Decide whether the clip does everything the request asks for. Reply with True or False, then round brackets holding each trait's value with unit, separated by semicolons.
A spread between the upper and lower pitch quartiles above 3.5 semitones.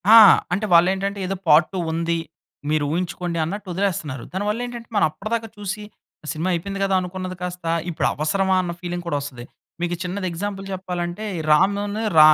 False (2.8 semitones)